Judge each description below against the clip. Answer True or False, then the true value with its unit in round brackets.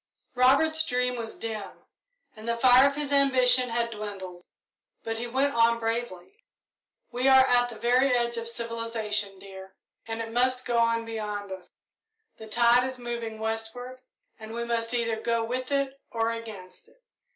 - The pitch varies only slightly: True (2.0 semitones)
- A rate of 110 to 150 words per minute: False (165 wpm)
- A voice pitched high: True (235 Hz)